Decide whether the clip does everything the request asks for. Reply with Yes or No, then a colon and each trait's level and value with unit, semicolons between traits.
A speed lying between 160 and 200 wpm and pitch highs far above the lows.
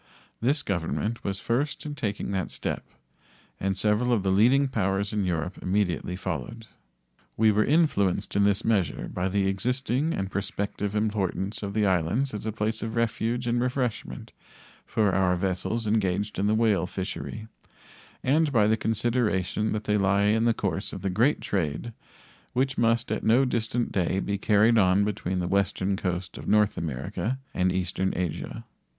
No: average, 170 wpm; average, 3.2 semitones